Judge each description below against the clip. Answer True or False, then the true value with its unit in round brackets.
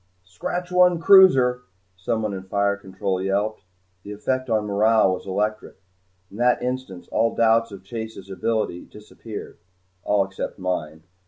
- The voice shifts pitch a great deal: False (3.4 semitones)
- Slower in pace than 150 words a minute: True (140 wpm)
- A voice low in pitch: True (105 Hz)